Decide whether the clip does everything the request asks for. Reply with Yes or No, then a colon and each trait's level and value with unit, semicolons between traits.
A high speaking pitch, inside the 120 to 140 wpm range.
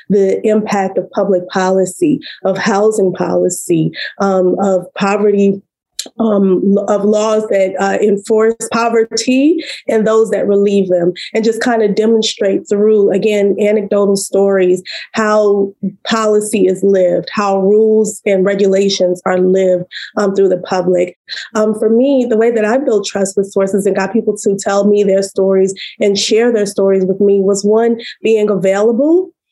No: high, 200 Hz; average, 150 wpm